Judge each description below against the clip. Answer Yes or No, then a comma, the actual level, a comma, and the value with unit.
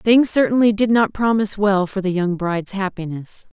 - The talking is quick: No, average, 185 wpm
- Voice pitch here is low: No, high, 200 Hz